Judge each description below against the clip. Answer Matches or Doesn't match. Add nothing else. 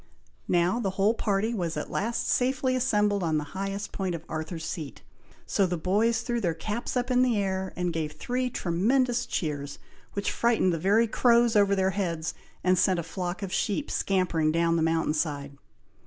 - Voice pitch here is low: Doesn't match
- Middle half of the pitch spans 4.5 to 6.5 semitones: Matches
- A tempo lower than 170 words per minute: Doesn't match